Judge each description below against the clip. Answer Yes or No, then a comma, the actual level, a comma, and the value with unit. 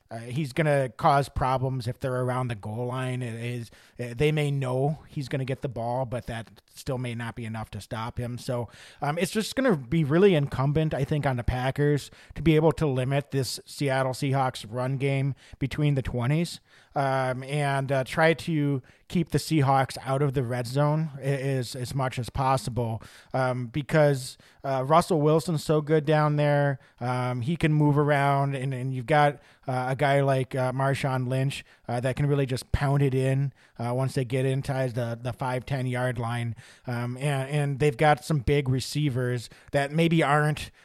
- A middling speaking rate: Yes, average, 195 wpm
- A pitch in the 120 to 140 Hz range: Yes, low, 135 Hz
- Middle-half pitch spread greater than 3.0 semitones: No, average, 2.7 semitones